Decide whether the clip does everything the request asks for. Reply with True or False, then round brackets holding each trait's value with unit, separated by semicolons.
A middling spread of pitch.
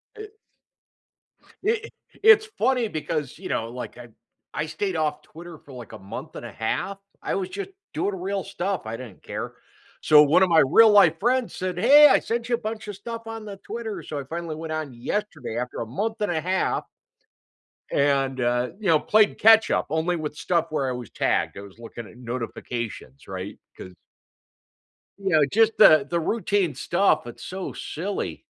False (8.0 semitones)